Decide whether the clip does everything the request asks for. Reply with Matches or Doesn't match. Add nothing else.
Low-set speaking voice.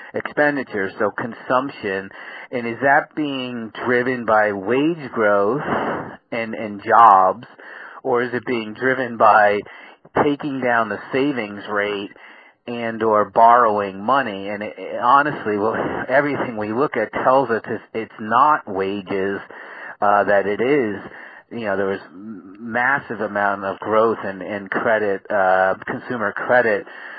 Matches